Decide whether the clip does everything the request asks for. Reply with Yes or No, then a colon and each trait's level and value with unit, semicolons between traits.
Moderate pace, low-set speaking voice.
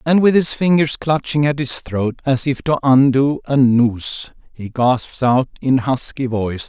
Yes: average, 180 wpm; low, 130 Hz